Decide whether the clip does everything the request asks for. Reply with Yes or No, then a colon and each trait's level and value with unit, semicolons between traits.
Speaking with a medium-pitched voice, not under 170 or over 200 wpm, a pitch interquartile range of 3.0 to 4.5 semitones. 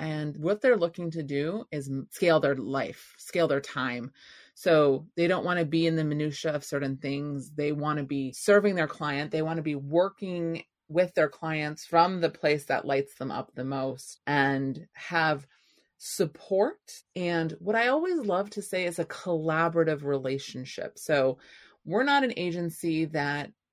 Yes: medium, 160 Hz; average, 175 wpm; average, 3.6 semitones